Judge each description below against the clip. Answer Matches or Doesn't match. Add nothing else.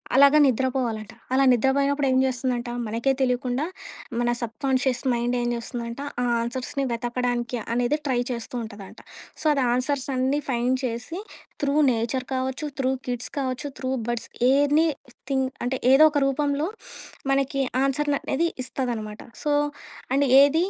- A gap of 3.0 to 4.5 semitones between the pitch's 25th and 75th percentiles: Doesn't match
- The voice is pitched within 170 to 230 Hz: Doesn't match